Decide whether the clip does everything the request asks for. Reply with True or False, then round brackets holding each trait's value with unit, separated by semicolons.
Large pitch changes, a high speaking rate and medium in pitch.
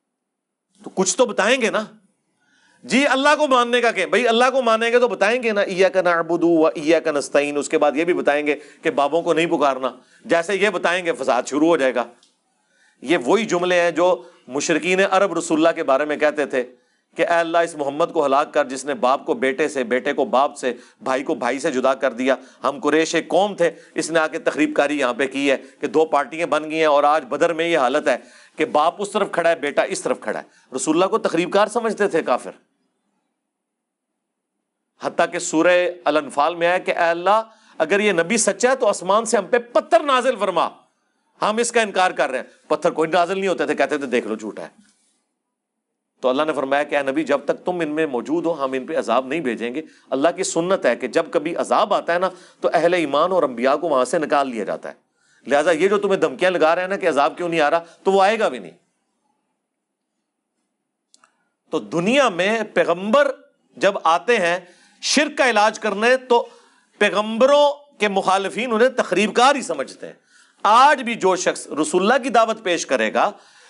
True (5.8 semitones; 215 wpm; 170 Hz)